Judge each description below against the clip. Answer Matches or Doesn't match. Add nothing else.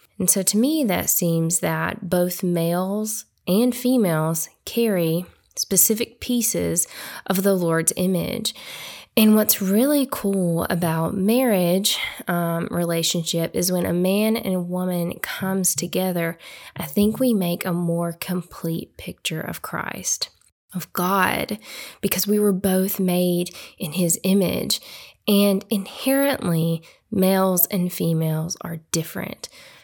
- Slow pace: Matches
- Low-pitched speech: Doesn't match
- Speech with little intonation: Doesn't match